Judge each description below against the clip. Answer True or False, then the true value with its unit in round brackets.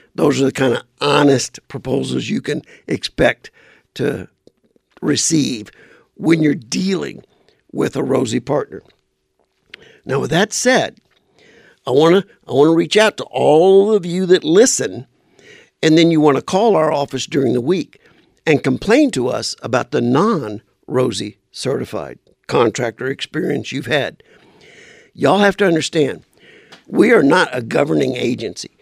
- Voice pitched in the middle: True (165 Hz)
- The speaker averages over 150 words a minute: False (145 wpm)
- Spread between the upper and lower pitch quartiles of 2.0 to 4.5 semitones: False (5.1 semitones)